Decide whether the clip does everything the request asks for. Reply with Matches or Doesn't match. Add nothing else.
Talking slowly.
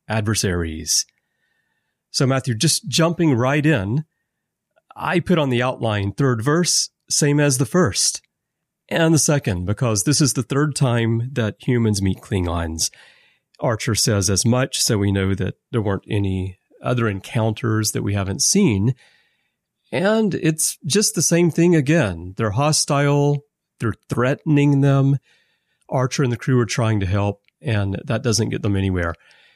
Doesn't match